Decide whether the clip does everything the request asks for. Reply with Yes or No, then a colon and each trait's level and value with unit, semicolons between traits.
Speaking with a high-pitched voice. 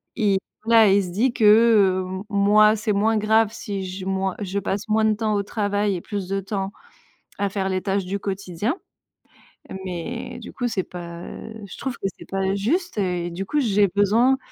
Yes: high, 200 Hz